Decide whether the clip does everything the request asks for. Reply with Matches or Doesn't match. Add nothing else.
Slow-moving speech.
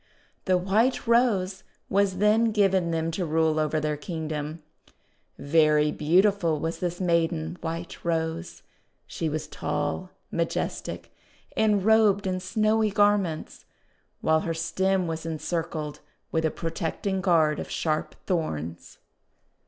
Matches